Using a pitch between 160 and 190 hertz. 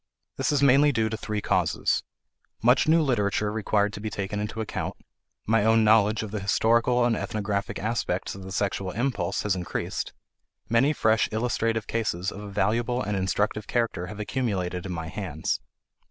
No: low, 105 Hz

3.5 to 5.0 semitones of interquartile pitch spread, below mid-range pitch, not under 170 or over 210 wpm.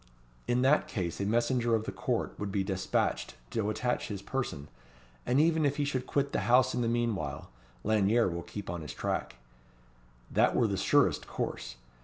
Yes: average, 4.6 semitones; low, 115 Hz; average, 185 wpm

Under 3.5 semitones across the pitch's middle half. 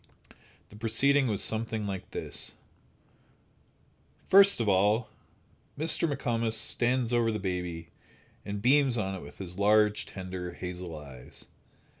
No: average, 4.3 semitones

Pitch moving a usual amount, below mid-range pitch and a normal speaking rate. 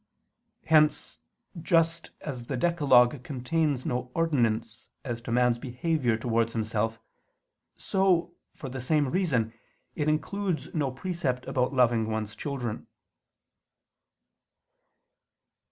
No: average, 5.0 semitones; low, 130 Hz; slow, 105 wpm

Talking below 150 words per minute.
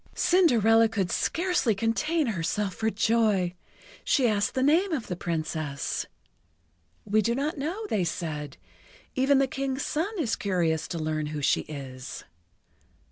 Yes: average, 140 wpm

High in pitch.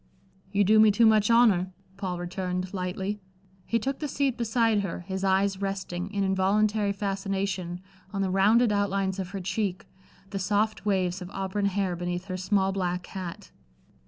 Yes: high, 195 Hz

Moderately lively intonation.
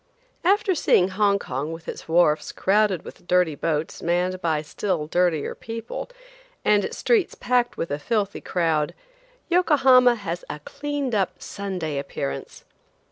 No: wide, 6.5 semitones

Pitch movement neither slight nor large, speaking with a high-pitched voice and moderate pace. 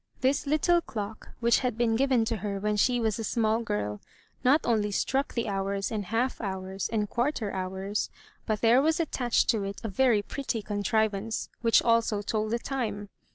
Yes: average, 3.0 semitones; high, 220 Hz; average, 185 wpm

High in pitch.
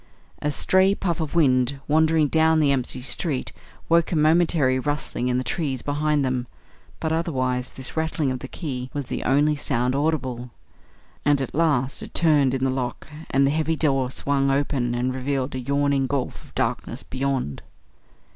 No: medium, 140 Hz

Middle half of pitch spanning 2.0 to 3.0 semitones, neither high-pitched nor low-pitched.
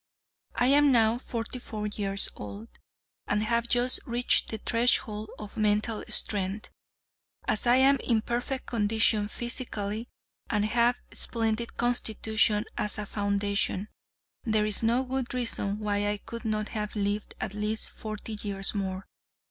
No: narrow, 2.4 semitones; high, 215 Hz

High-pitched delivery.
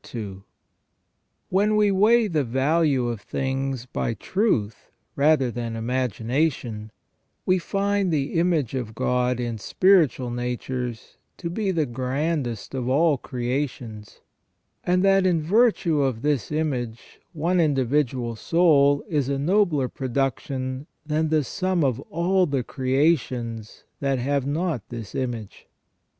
No: low, 135 Hz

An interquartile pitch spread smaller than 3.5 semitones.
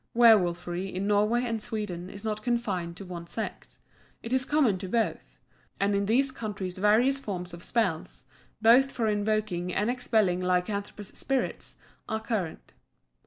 No: average, 4.0 semitones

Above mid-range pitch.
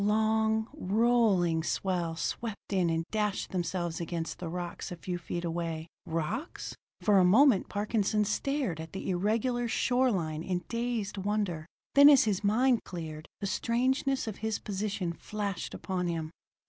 Yes: high, 200 Hz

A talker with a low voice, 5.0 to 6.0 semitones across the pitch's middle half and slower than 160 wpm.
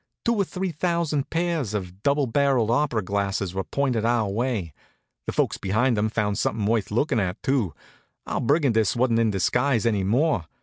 No: low, 115 Hz; wide, 5.5 semitones; average, 175 wpm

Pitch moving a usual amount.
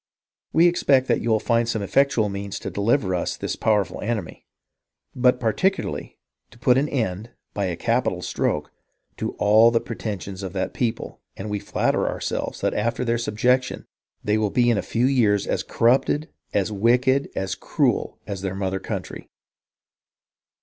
Yes: average, 3.7 semitones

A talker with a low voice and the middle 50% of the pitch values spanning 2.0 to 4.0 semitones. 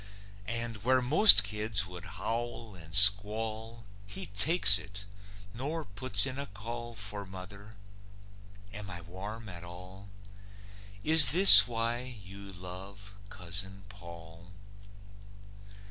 Yes: low, 100 Hz; average, 3.6 semitones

